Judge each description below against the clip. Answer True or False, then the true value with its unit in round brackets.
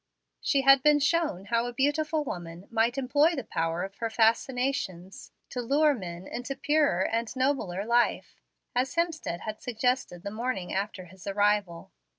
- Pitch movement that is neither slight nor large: False (6.0 semitones)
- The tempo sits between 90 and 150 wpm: False (160 wpm)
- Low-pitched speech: False (235 Hz)